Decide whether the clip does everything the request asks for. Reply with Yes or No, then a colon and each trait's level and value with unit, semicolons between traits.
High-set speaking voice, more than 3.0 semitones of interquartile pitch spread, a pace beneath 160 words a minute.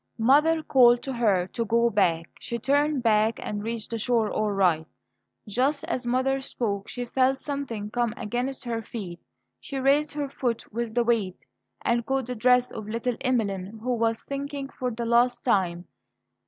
No: high, 235 Hz; average, 3.4 semitones; average, 175 wpm